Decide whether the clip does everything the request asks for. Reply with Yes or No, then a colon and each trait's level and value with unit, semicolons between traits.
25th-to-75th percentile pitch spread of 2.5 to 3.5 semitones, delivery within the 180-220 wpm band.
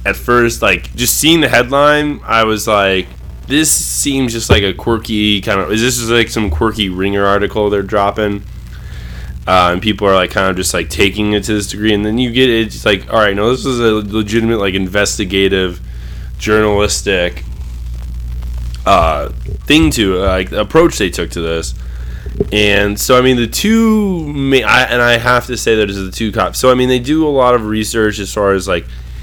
No: average, 4.3 semitones; fast, 205 wpm